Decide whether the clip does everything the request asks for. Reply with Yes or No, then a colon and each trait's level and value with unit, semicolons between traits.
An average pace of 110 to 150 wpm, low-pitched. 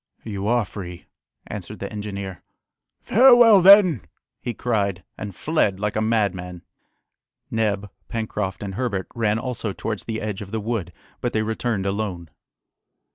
Yes: average, 140 wpm; low, 105 Hz